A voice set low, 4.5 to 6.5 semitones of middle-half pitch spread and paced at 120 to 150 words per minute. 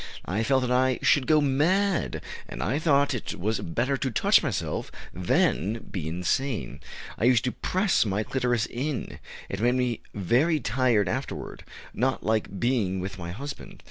No: low, 120 Hz; average, 4.9 semitones; average, 165 wpm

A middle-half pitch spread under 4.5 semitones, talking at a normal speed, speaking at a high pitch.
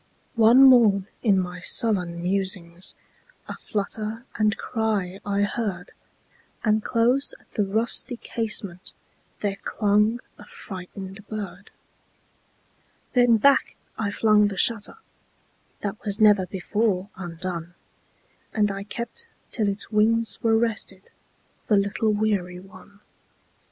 No: average, 2.7 semitones; slow, 100 wpm; high, 205 Hz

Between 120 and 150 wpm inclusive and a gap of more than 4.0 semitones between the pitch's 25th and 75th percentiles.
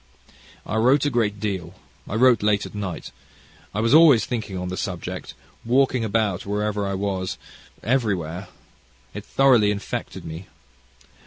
No: average, 145 wpm; average, 3.5 semitones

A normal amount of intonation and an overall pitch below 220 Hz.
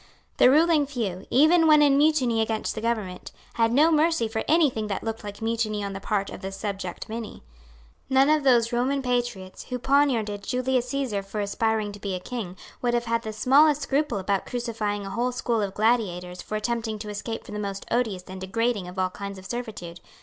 No: average, 3.8 semitones; high, 225 Hz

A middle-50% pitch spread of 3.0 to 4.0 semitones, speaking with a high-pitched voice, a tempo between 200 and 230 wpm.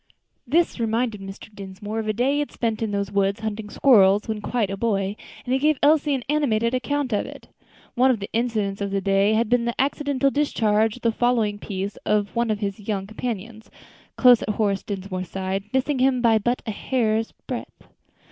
Yes: average, 3.6 semitones; high, 220 Hz; fast, 205 wpm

